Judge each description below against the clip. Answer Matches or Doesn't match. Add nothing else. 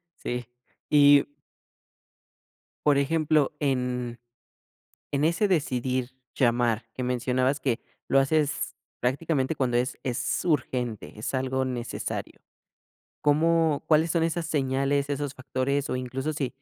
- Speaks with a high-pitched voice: Doesn't match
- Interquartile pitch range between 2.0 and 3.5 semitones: Matches